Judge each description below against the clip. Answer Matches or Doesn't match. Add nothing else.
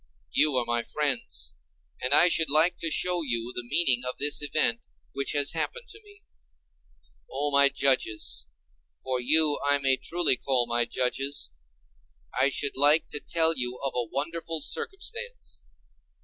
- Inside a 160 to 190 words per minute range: Doesn't match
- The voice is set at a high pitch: Doesn't match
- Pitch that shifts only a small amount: Doesn't match